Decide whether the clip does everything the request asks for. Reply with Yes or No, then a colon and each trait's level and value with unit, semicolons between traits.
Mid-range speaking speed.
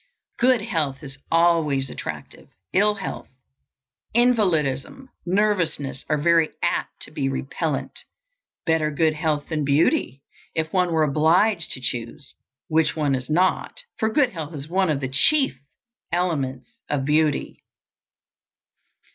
No: slow, 130 wpm